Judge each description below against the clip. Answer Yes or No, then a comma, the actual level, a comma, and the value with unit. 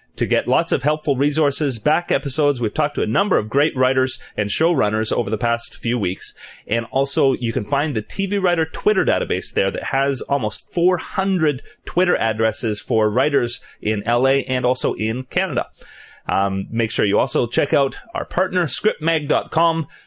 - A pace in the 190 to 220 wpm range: No, average, 175 wpm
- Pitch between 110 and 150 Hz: Yes, low, 135 Hz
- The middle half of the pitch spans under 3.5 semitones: No, average, 5.0 semitones